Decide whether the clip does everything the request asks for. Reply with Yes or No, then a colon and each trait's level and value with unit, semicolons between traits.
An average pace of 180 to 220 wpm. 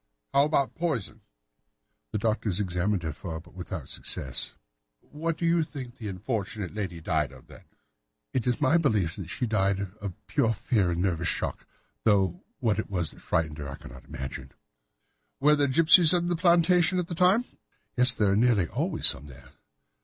Yes: average, 185 wpm